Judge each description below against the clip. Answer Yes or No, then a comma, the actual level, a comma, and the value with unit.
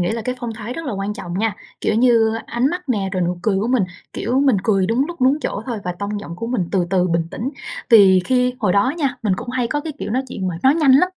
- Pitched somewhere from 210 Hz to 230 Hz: Yes, high, 225 Hz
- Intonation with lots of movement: No, average, 4.9 semitones